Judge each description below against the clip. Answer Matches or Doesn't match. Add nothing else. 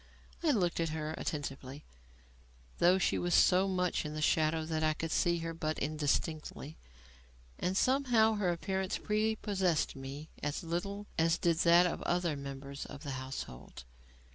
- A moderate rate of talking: Matches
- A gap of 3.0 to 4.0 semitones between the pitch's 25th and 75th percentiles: Matches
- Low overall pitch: Doesn't match